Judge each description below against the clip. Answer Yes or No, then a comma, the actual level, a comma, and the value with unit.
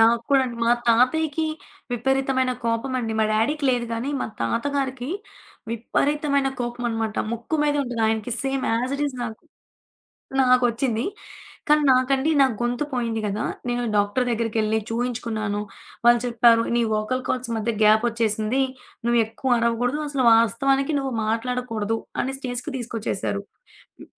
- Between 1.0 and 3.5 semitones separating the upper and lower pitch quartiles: Yes, average, 2.8 semitones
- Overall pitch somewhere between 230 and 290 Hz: Yes, high, 240 Hz